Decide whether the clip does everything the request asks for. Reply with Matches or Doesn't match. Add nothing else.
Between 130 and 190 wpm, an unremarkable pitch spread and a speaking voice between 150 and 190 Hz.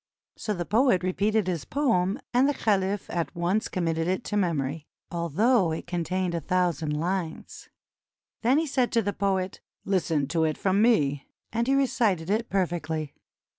Matches